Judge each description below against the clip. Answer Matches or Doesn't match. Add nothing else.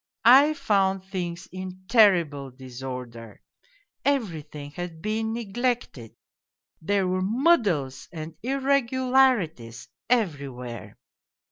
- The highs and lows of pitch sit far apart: Matches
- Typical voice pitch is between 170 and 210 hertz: Matches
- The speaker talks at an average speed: Doesn't match